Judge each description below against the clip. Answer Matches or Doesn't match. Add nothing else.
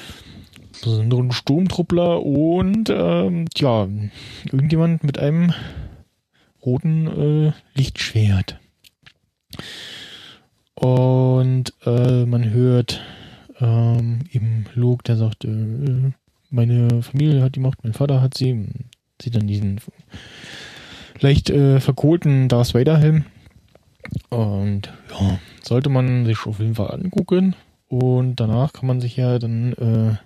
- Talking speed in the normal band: Doesn't match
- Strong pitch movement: Doesn't match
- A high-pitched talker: Doesn't match